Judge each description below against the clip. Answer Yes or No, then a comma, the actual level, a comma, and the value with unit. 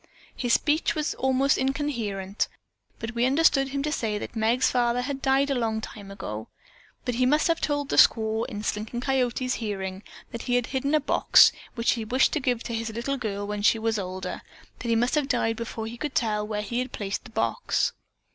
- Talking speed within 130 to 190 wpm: No, average, 200 wpm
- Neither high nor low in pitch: No, high, 235 Hz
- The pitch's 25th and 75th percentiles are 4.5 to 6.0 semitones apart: No, average, 3.6 semitones